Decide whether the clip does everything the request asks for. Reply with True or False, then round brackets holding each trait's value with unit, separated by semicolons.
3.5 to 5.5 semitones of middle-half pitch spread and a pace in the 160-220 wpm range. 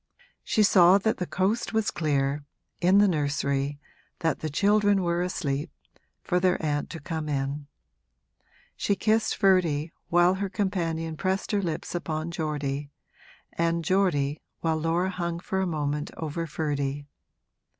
False (4.1 semitones; 140 wpm)